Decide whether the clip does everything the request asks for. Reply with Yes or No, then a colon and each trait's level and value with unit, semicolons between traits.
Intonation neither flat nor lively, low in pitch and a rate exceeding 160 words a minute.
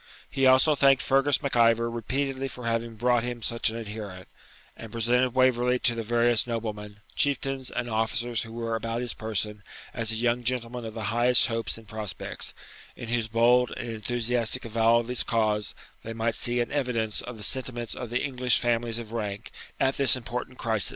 No: narrow, 1.7 semitones; low, 115 Hz; average, 190 wpm